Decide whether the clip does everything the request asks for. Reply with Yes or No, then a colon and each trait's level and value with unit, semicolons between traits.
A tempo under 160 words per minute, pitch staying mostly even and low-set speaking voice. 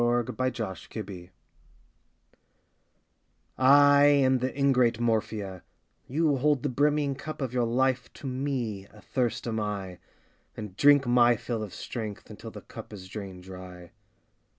No: average, 140 wpm; average, 4.3 semitones; low, 120 Hz